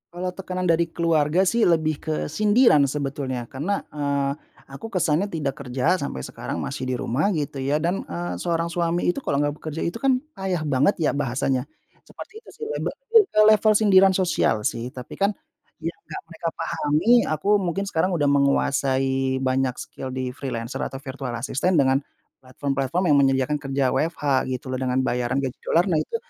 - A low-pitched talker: No, medium, 145 Hz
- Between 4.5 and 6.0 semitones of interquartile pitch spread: Yes, average, 4.8 semitones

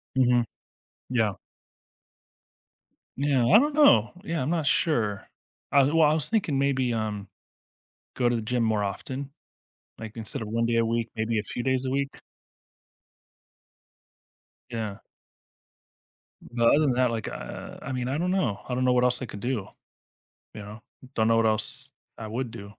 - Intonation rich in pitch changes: No, average, 3.5 semitones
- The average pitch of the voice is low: Yes, low, 120 Hz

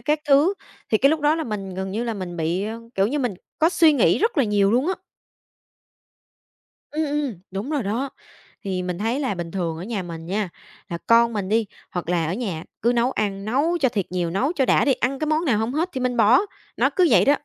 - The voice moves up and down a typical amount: No, wide, 6.6 semitones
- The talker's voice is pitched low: No, high, 230 Hz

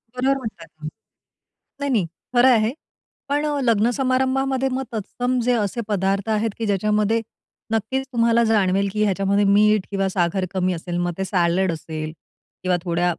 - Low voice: No, high, 210 Hz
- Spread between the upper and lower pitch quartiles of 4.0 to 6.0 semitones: Yes, average, 4.7 semitones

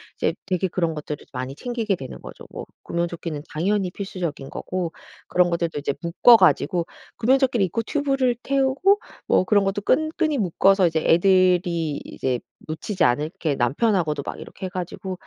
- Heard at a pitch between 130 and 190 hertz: Yes, medium, 185 Hz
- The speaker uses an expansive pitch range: No, average, 4.8 semitones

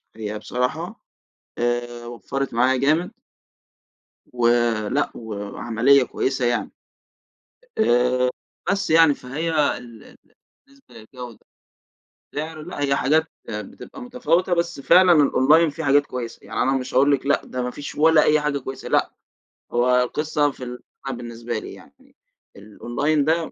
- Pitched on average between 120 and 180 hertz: Yes, low, 135 Hz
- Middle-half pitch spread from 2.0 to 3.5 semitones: No, average, 4.5 semitones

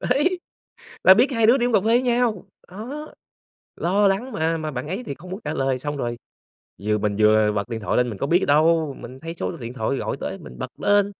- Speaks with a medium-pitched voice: Yes, medium, 165 Hz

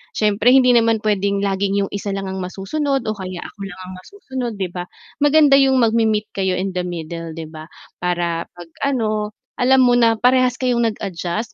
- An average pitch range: Yes, average, 4.9 semitones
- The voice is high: Yes, high, 210 Hz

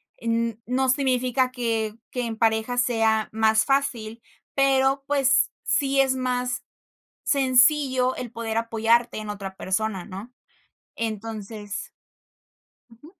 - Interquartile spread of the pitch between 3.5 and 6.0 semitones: No, average, 2.9 semitones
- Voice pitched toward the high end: Yes, high, 235 Hz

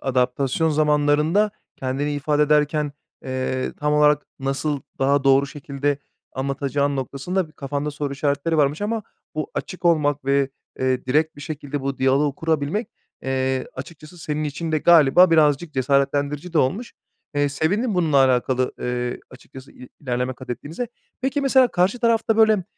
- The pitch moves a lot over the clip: No, average, 2.8 semitones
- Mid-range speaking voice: Yes, medium, 145 Hz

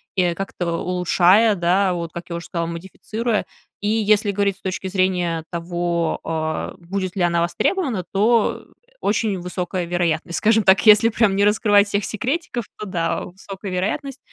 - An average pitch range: Yes, average, 3.2 semitones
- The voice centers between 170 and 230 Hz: Yes, high, 190 Hz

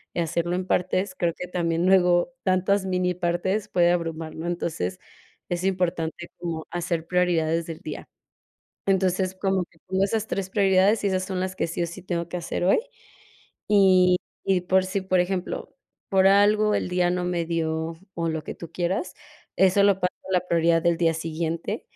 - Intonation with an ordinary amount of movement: No, narrow, 1.9 semitones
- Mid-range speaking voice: Yes, medium, 180 Hz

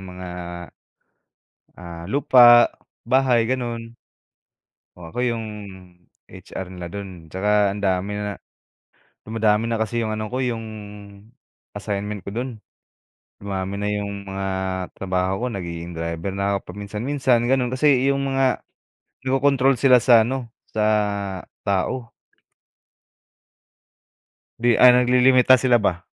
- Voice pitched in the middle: No, low, 110 Hz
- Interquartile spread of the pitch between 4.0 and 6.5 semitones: Yes, average, 4.3 semitones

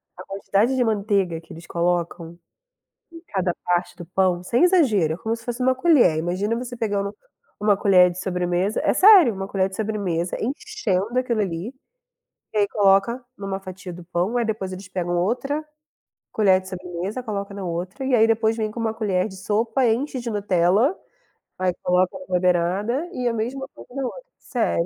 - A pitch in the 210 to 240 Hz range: No, high, 200 Hz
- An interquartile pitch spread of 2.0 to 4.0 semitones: No, average, 4.6 semitones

